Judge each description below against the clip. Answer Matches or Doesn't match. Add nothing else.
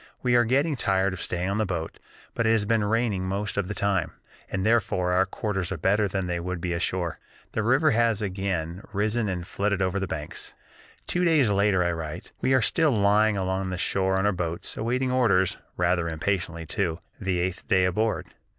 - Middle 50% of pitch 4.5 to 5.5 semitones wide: Doesn't match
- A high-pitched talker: Doesn't match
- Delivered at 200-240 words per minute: Matches